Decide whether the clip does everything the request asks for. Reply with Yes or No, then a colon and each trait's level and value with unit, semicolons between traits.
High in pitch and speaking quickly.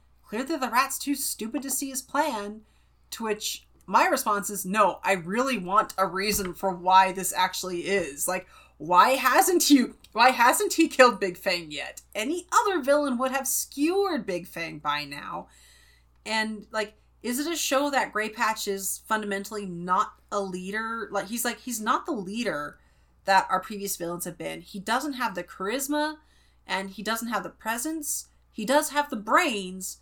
No: high, 215 Hz; average, 180 wpm